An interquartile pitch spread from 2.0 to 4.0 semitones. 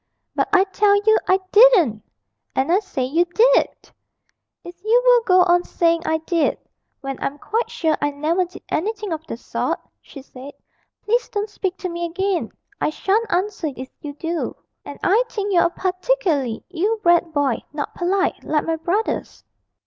No: average, 4.5 semitones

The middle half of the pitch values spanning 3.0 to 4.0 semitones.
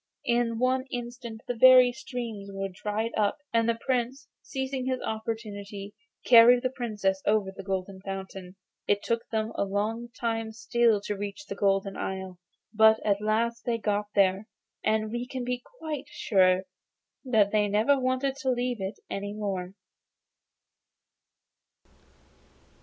Yes: average, 3.4 semitones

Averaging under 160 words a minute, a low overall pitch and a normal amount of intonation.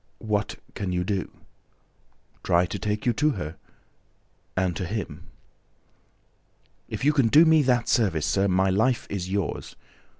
Yes: average, 145 wpm; low, 100 Hz; average, 4.7 semitones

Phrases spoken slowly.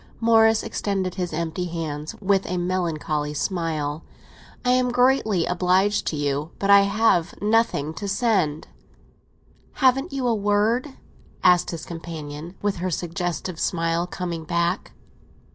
Yes: slow, 130 wpm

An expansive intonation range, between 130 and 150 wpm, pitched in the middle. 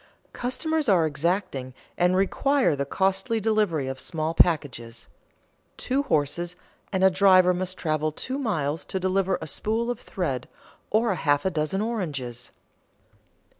Yes: wide, 5.8 semitones; slow, 135 wpm; medium, 180 Hz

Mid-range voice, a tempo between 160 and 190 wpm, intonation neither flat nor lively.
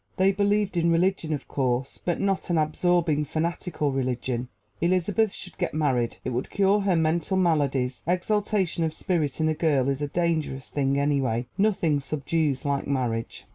Yes: medium, 155 Hz; average, 165 wpm; average, 4.7 semitones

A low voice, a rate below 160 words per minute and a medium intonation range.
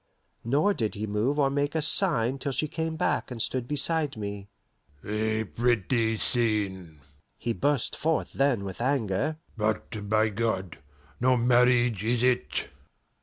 Yes: low, 120 Hz; average, 145 wpm; average, 4.5 semitones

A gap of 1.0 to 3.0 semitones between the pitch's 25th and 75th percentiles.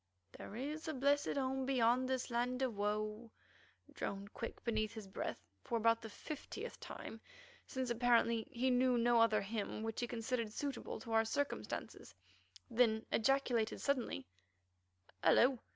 Yes: average, 2.7 semitones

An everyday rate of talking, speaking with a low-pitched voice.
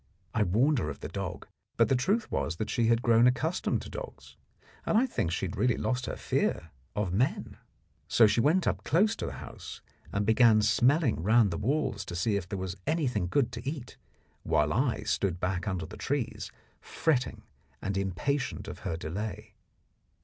Yes: average, 185 wpm; low, 115 Hz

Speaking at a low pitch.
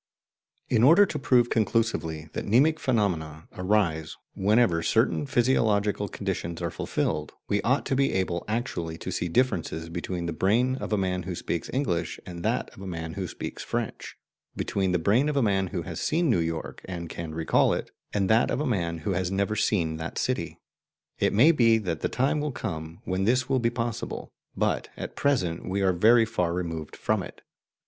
Yes: very low, 95 Hz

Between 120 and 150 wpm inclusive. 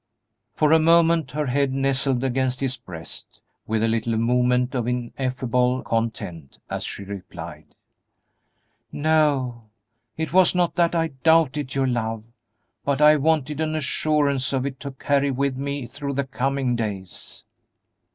Yes: average, 140 wpm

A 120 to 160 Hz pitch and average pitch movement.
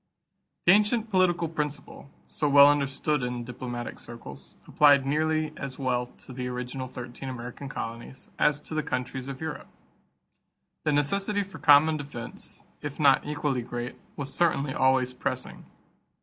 Yes: medium, 140 Hz; average, 3.2 semitones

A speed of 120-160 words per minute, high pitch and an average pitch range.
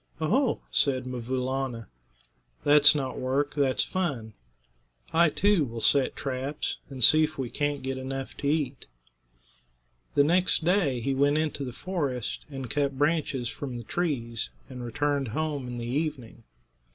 No: average, 150 wpm; medium, 140 Hz; average, 3.0 semitones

